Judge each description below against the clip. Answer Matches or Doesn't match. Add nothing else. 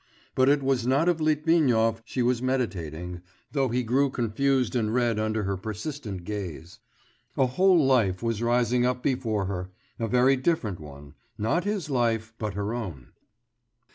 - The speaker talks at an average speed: Matches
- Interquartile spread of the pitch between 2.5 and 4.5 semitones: Matches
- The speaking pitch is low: Matches